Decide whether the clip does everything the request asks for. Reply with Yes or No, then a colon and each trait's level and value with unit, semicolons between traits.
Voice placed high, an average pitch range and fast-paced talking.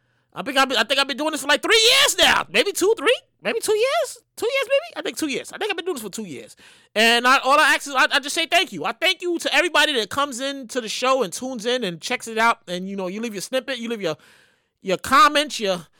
No: very high, 275 Hz; wide, 6.1 semitones; fast, 295 wpm